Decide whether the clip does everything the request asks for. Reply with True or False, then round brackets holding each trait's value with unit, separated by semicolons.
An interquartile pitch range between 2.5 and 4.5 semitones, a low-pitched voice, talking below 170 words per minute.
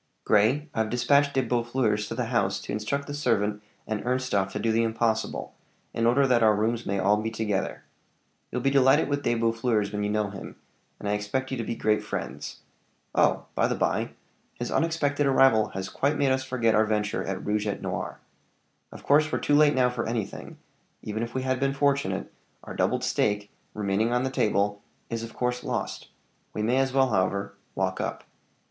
False (3.9 semitones; 115 Hz; 200 wpm)